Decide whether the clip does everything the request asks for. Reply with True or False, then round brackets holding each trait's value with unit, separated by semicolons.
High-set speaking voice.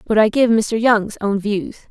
True (215 Hz)